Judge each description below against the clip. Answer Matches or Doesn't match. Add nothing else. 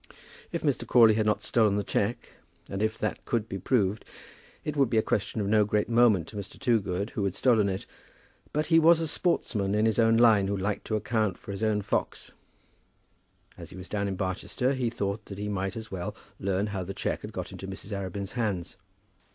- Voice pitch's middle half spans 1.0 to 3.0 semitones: Matches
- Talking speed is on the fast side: Matches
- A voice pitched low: Matches